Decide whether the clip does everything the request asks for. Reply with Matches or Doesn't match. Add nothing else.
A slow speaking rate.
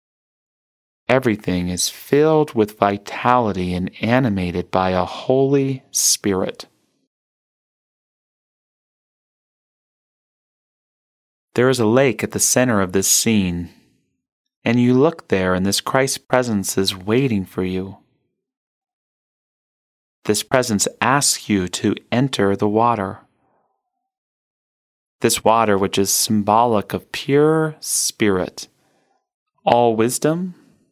Matches